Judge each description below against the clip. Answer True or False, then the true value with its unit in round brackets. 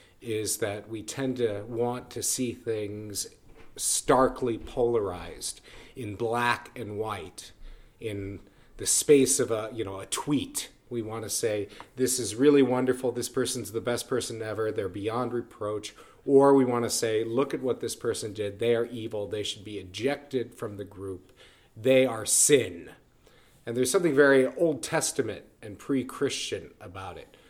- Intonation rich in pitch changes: False (3.4 semitones)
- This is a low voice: True (115 Hz)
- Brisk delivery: False (165 wpm)